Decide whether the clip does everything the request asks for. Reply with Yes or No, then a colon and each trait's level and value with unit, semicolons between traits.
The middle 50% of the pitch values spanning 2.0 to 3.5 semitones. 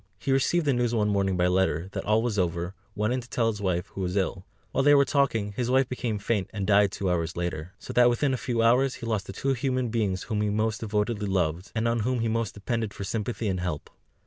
No: average, 4.0 semitones